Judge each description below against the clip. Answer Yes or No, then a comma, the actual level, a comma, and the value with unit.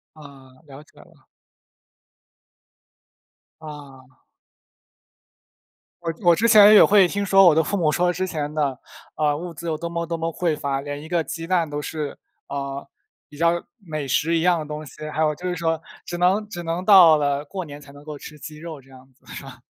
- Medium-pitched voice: Yes, medium, 160 Hz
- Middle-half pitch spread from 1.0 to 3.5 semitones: Yes, average, 3.0 semitones